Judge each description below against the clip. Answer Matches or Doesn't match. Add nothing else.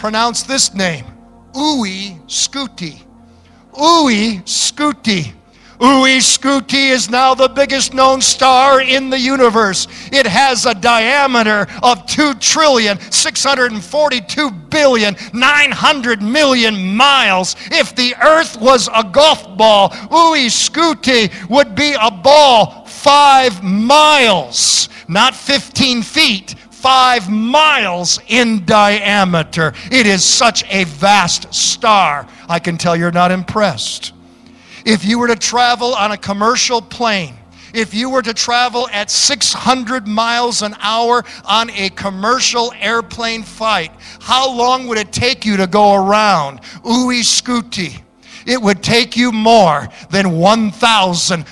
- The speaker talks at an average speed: Doesn't match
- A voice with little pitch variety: Doesn't match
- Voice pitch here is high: Matches